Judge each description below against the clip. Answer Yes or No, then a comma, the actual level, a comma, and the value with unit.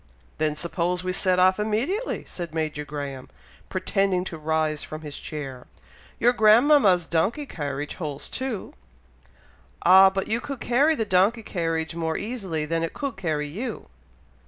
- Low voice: No, medium, 180 Hz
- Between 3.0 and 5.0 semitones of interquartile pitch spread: No, wide, 5.6 semitones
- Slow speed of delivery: No, average, 150 wpm